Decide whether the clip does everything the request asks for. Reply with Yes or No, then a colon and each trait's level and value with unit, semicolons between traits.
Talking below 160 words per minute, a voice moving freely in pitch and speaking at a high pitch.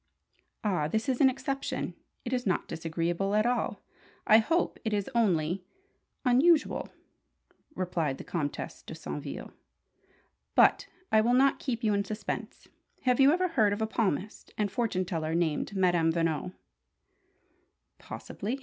Yes: average, 140 wpm; wide, 6.1 semitones; high, 210 Hz